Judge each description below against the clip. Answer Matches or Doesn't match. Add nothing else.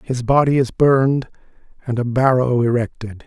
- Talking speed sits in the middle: Matches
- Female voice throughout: Doesn't match